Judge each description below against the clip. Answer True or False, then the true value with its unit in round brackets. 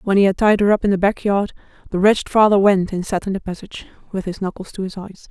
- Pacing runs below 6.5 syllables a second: False (6.6 syllables/s)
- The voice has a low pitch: False (195 Hz)